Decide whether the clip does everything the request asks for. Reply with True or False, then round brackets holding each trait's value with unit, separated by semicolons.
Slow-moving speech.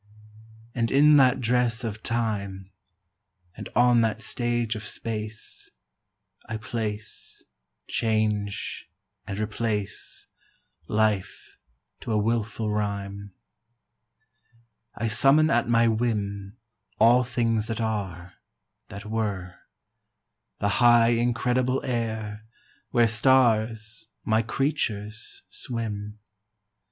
True (95 wpm)